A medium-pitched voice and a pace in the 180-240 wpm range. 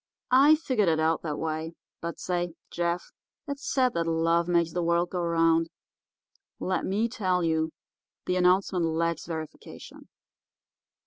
No: medium, 170 Hz; average, 140 wpm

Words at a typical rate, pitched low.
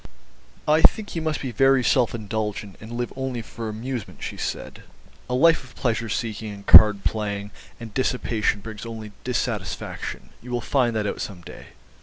Yes: average, 175 wpm; low, 115 Hz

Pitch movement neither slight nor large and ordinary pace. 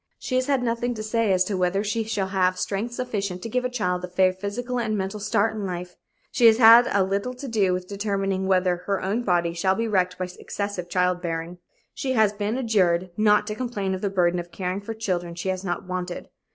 No: average, 3.4 semitones; fast, 230 wpm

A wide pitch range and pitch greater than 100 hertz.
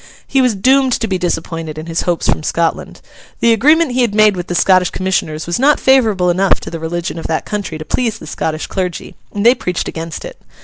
Yes: wide, 5.9 semitones; medium, 185 Hz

